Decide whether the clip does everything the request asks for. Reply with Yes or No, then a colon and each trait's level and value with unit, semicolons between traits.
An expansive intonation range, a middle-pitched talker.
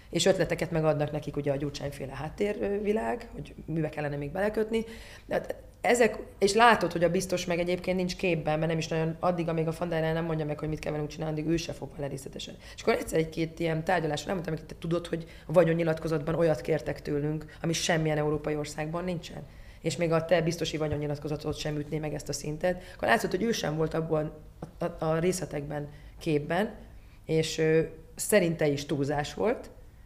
No: narrow, 2.4 semitones; medium, 160 Hz